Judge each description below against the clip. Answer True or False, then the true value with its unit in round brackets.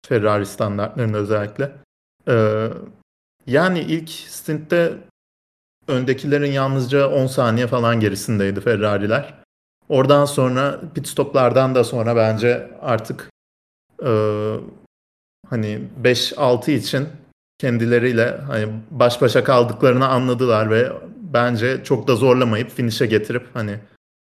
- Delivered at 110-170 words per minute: False (100 wpm)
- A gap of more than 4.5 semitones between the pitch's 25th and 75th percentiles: False (3.9 semitones)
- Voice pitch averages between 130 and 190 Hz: False (120 Hz)